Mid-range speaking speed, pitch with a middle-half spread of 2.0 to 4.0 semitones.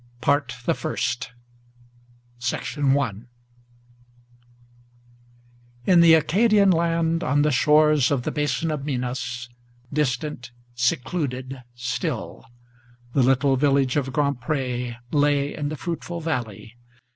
No: slow, 105 wpm; average, 3.4 semitones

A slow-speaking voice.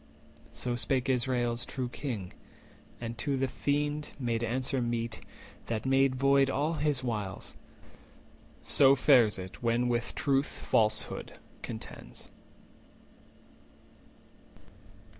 Yes: slow, 105 wpm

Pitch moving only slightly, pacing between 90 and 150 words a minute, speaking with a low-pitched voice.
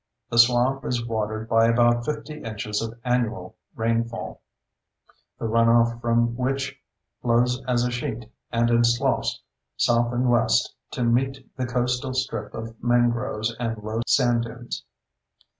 Yes: narrow, 1.3 semitones; average, 140 wpm; low, 120 Hz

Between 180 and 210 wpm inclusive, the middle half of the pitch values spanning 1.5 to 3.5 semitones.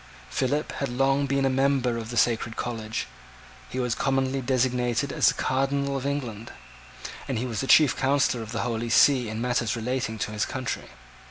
Yes: average, 185 wpm; average, 2.7 semitones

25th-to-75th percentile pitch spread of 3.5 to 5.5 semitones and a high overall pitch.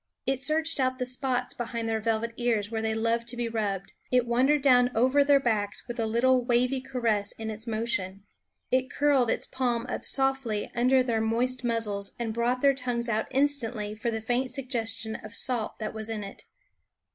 No: narrow, 2.5 semitones; high, 235 Hz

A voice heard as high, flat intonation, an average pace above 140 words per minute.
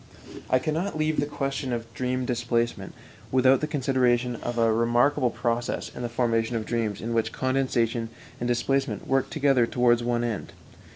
No: low, 120 Hz; narrow, 2.1 semitones; average, 165 wpm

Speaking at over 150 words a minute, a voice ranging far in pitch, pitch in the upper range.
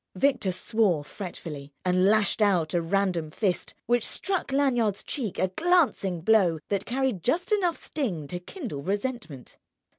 No: average, 145 wpm; wide, 6.5 semitones; high, 200 Hz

